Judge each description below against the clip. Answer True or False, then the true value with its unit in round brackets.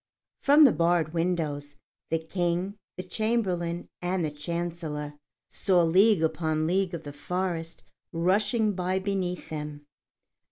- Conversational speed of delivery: False (125 wpm)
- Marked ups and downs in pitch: False (2.8 semitones)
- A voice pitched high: False (175 Hz)